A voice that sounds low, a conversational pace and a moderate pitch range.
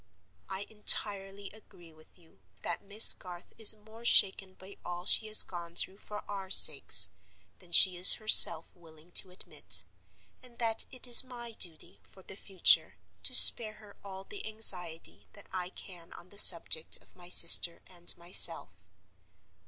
No: high, 190 Hz; average, 160 wpm; average, 3.4 semitones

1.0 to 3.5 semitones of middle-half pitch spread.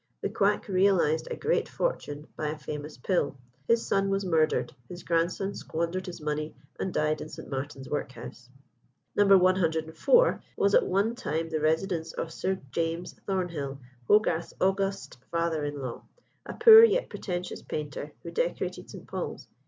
No: average, 4.2 semitones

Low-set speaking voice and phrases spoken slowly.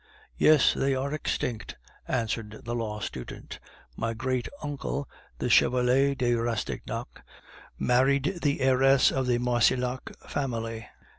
Yes: low, 125 Hz; slow, 120 wpm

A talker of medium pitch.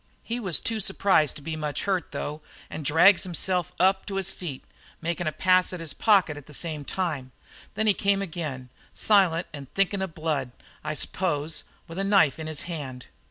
Yes: medium, 165 Hz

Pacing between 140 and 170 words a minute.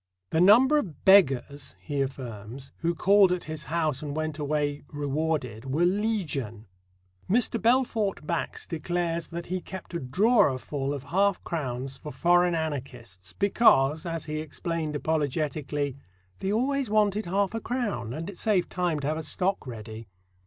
Yes: average, 150 wpm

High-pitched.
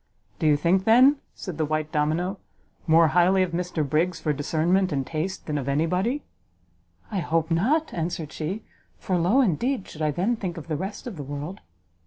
No: medium, 170 Hz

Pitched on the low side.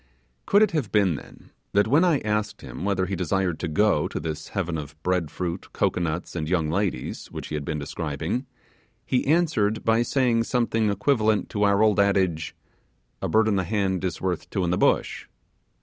Yes: low, 100 Hz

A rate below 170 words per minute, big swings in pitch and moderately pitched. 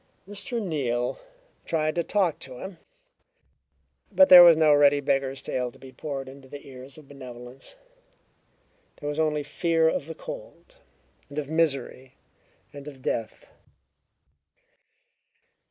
No: slow, 135 wpm; average, 3.6 semitones; medium, 145 Hz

